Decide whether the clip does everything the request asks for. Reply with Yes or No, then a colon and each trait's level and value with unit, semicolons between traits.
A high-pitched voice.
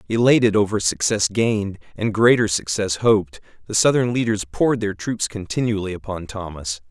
No: low, 105 Hz